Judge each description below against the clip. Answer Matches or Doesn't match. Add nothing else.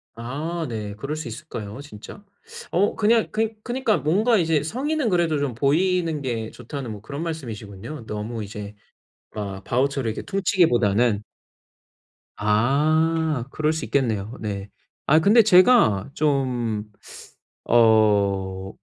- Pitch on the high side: Doesn't match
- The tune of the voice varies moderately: Doesn't match